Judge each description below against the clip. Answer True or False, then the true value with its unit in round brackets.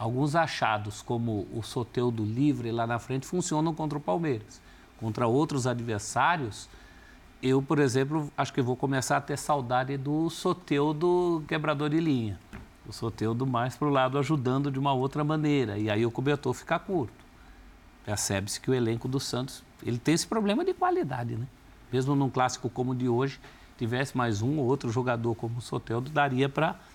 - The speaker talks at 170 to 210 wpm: True (175 wpm)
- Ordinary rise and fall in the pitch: True (3.7 semitones)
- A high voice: False (130 Hz)